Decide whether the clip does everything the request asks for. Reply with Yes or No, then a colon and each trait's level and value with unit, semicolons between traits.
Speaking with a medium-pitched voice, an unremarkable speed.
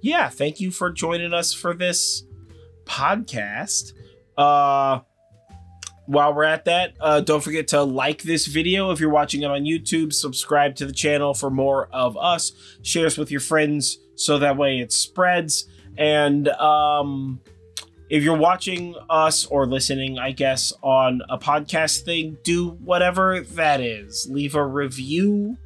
Yes: medium, 145 Hz; average, 155 wpm